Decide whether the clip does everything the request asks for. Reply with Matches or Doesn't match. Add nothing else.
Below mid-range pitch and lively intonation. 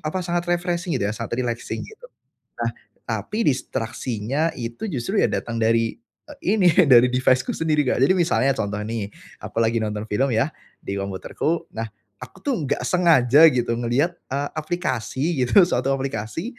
Matches